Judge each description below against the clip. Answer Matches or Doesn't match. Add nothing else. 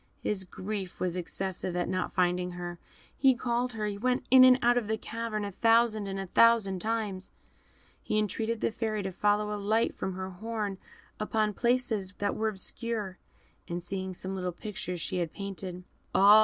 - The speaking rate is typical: Matches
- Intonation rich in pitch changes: Doesn't match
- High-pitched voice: Matches